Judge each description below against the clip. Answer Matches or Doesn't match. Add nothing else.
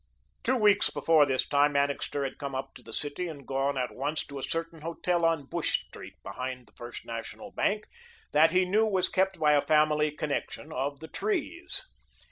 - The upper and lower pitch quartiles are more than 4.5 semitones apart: Doesn't match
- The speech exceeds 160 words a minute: Matches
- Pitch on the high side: Doesn't match